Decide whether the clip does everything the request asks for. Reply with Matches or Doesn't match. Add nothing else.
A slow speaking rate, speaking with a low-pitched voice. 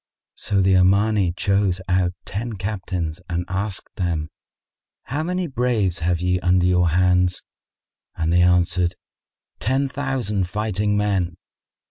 Matches